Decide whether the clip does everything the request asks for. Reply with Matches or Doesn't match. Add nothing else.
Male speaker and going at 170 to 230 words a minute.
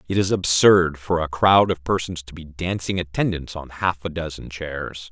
Matches